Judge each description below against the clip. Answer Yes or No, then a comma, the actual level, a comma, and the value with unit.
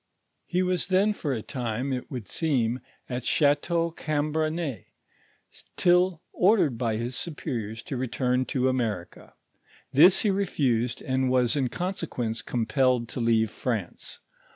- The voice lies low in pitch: Yes, low, 130 Hz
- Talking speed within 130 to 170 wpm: Yes, average, 140 wpm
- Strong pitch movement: Yes, wide, 5.7 semitones